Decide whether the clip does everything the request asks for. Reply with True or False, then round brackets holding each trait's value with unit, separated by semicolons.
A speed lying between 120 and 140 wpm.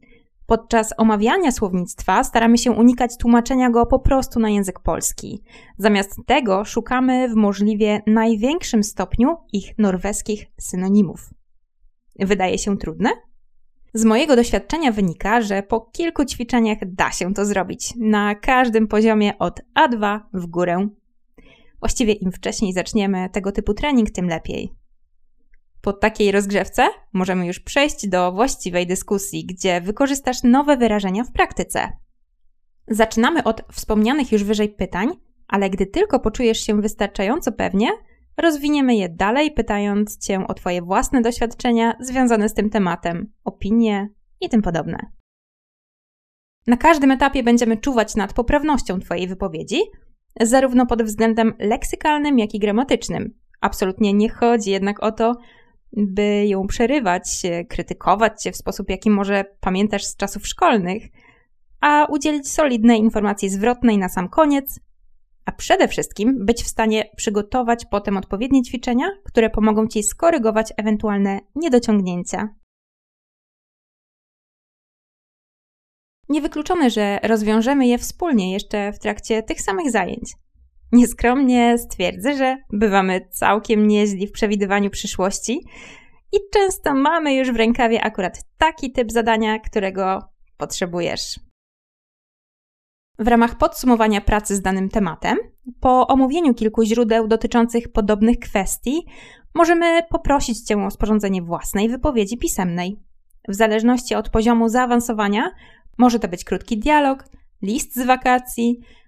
True (125 wpm)